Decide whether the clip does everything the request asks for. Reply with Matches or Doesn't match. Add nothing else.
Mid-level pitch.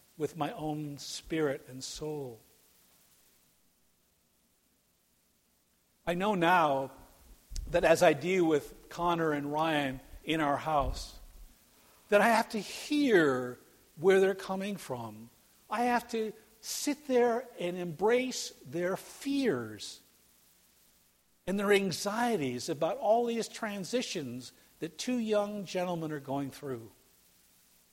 Matches